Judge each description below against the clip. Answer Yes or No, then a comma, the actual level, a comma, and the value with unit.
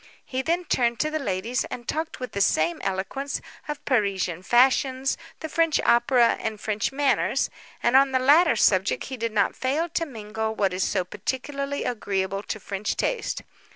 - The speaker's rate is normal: Yes, average, 175 wpm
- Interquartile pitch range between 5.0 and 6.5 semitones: Yes, wide, 5.4 semitones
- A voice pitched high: Yes, high, 240 Hz